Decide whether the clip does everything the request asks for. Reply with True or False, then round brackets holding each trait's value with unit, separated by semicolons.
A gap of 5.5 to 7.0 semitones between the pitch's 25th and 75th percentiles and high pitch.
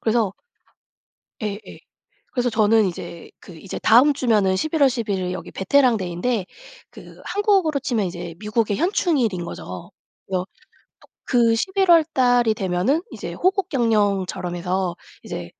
True (6.3 semitones; 220 Hz)